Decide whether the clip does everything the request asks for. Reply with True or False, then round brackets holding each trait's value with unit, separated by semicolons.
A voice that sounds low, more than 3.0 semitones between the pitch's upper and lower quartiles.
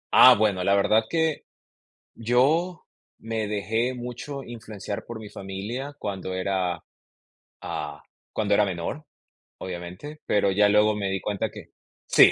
True (105 Hz; 4.0 semitones)